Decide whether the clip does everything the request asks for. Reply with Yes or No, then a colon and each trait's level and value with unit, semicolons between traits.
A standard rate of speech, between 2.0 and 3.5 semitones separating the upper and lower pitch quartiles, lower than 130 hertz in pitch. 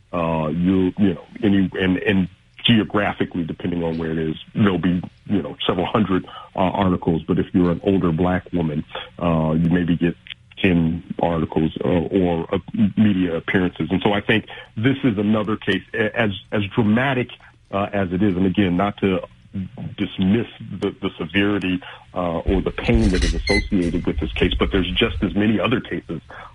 Yes: average, 180 wpm; average, 3.1 semitones; very low, 95 Hz